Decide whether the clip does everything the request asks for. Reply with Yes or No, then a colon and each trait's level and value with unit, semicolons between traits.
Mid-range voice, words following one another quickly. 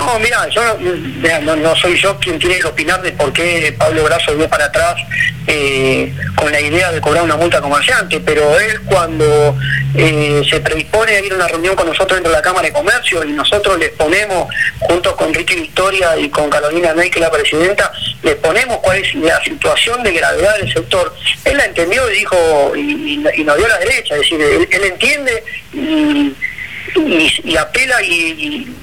Yes: medium, 175 Hz; fast, 200 wpm